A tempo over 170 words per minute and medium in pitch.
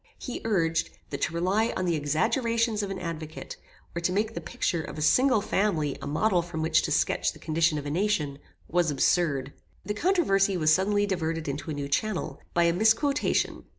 Yes: average, 195 wpm; medium, 175 Hz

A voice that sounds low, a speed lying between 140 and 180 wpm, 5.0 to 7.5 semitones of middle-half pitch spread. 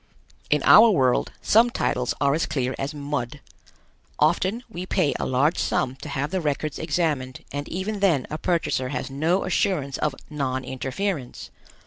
No: medium, 145 Hz; average, 160 wpm; average, 5.3 semitones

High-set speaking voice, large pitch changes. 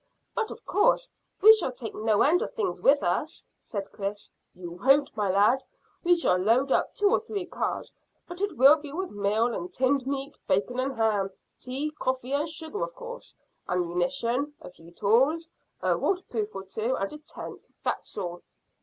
Yes: very high, 260 Hz; wide, 7.8 semitones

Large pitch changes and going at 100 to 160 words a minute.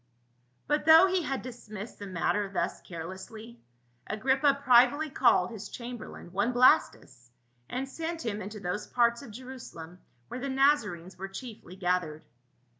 Yes: wide, 5.8 semitones; average, 145 wpm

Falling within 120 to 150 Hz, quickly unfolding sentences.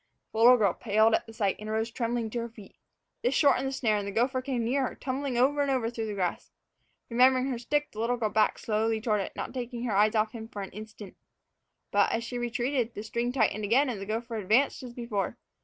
No: high, 230 Hz; fast, 240 wpm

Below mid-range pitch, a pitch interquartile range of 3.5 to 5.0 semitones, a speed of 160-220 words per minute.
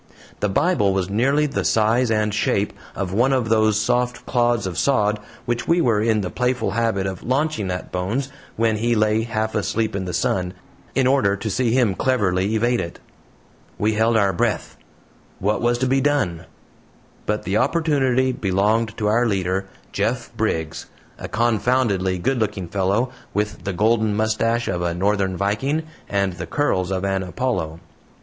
Yes: low, 110 Hz; average, 3.8 semitones; average, 170 wpm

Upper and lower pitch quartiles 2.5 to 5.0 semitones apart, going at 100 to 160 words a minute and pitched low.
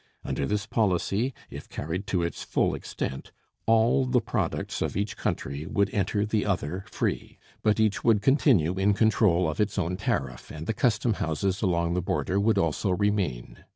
No: average, 4.2 semitones; average, 170 wpm; low, 100 Hz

